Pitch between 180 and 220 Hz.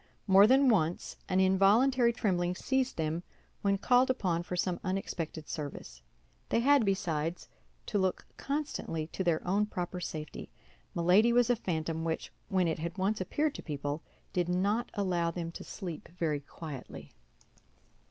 Yes: medium, 185 Hz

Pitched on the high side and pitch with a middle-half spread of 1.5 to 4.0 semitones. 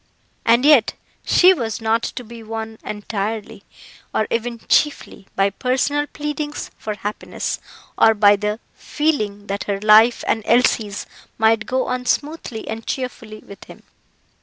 Yes: high, 225 Hz; average, 3.1 semitones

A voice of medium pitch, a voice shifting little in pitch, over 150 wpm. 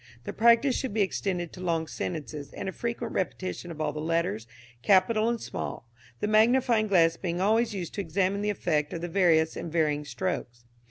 No: medium, 180 Hz; average, 4.7 semitones; average, 195 wpm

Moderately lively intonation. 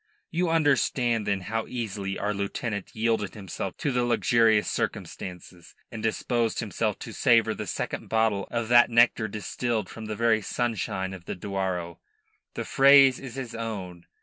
Yes: average, 3.4 semitones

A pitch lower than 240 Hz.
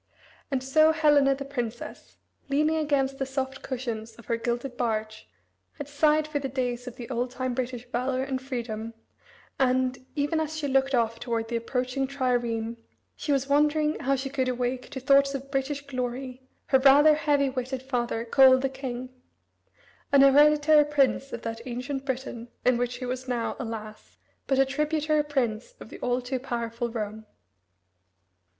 No: very high, 260 Hz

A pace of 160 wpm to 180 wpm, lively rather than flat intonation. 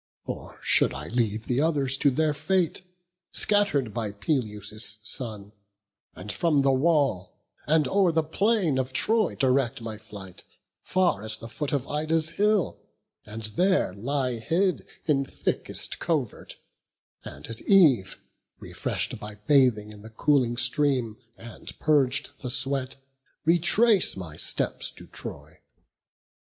No: slow, 135 wpm; wide, 6.3 semitones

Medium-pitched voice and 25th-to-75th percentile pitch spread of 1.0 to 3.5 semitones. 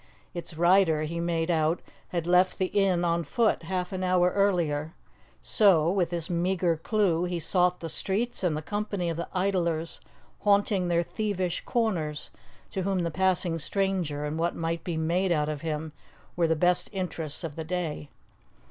Yes: medium, 175 Hz; narrow, 2.5 semitones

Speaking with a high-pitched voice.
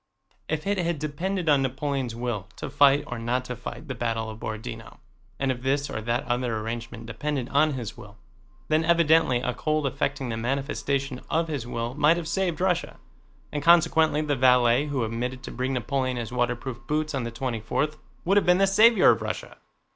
No: low, 135 Hz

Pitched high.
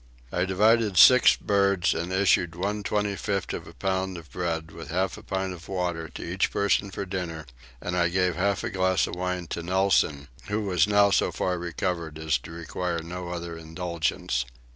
No: very low, 90 Hz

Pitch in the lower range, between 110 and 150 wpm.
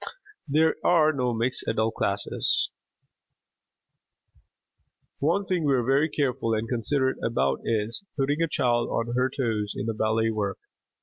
Yes: low, 125 Hz; average, 140 wpm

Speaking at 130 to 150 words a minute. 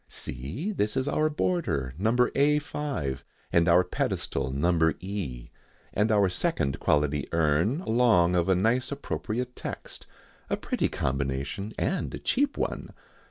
Yes: average, 140 wpm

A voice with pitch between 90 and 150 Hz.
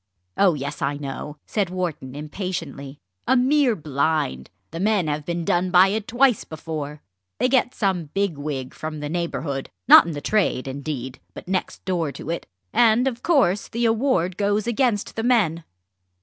No: medium, 175 Hz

